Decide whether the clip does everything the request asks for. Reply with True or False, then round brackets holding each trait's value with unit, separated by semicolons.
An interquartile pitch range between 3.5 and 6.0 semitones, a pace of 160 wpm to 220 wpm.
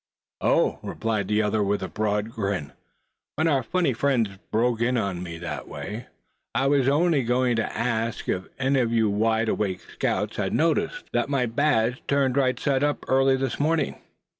True (4.2 semitones; 190 wpm)